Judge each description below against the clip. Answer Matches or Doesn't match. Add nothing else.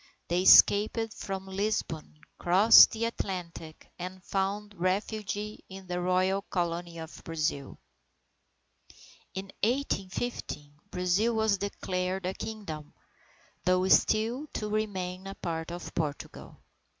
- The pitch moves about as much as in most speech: Matches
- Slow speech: Matches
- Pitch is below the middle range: Doesn't match